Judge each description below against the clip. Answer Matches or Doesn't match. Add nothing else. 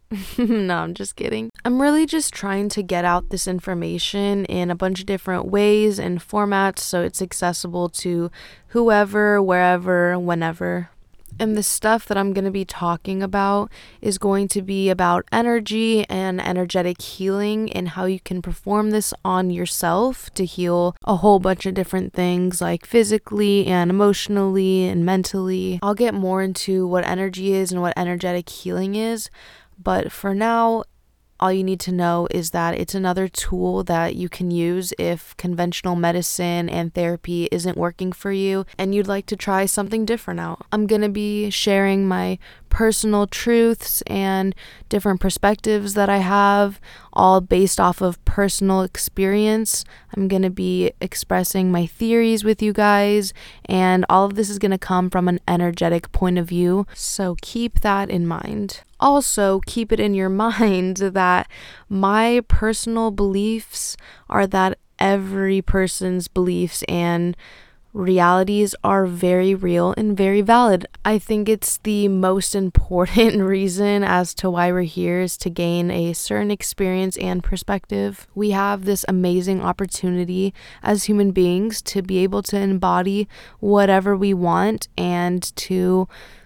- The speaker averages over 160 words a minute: Doesn't match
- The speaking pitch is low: Doesn't match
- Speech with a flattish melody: Matches